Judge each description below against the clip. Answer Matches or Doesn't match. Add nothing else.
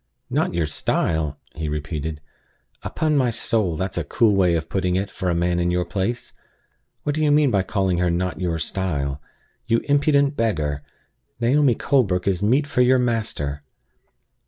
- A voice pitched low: Matches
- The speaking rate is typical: Matches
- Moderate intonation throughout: Doesn't match